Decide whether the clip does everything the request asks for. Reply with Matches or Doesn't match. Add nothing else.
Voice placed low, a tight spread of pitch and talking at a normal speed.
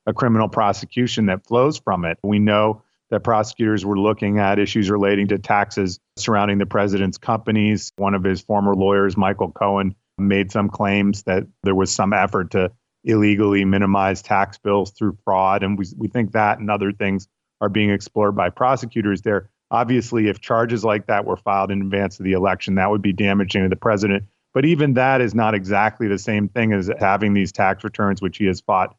Matches